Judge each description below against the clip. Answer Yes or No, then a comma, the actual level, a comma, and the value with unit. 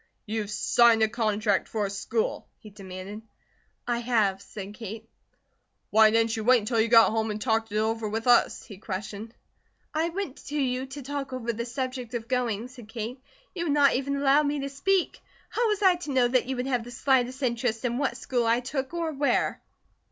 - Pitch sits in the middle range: No, high, 240 Hz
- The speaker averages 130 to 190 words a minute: No, fast, 205 wpm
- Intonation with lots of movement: No, average, 3.4 semitones